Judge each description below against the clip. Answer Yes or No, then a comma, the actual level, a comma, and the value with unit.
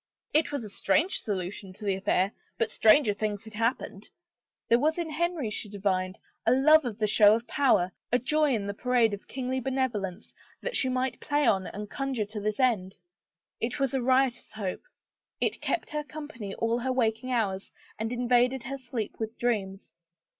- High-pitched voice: Yes, high, 235 Hz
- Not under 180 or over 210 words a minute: Yes, average, 185 wpm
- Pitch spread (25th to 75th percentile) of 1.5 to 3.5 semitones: No, average, 4.2 semitones